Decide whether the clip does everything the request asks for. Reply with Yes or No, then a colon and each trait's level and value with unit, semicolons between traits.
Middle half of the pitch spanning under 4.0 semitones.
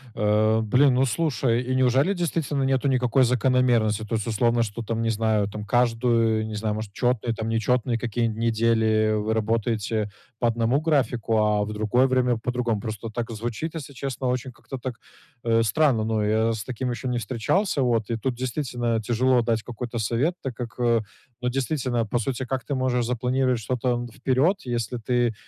Yes: narrow, 2.4 semitones